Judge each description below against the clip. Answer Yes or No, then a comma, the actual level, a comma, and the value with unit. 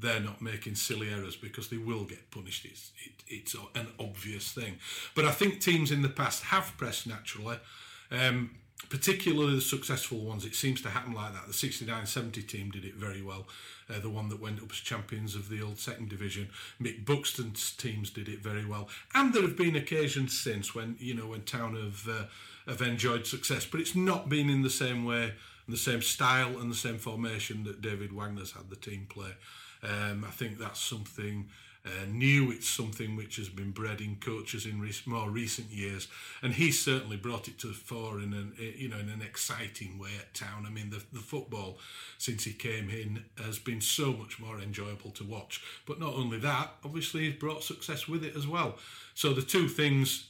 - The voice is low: Yes, low, 115 Hz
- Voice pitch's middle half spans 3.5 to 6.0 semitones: Yes, average, 3.8 semitones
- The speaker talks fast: Yes, fast, 210 wpm